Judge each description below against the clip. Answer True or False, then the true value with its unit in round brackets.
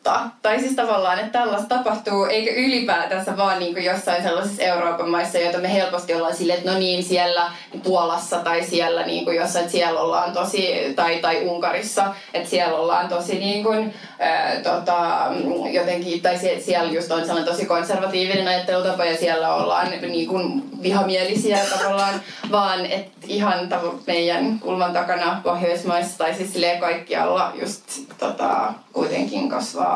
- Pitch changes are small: True (2.3 semitones)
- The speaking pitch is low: False (180 Hz)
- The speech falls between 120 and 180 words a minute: True (150 wpm)